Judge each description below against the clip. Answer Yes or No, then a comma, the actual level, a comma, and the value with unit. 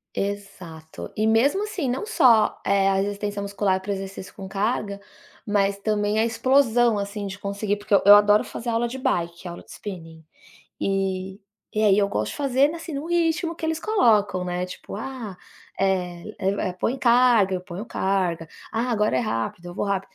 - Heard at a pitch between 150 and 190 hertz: No, high, 205 Hz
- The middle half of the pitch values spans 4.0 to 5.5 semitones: No, average, 3.5 semitones